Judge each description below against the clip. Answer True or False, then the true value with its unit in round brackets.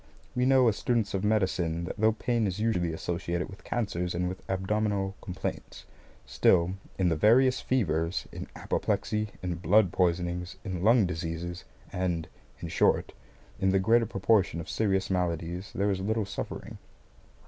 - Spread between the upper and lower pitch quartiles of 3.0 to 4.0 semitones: True (3.6 semitones)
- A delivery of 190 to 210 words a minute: False (155 wpm)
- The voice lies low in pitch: True (95 Hz)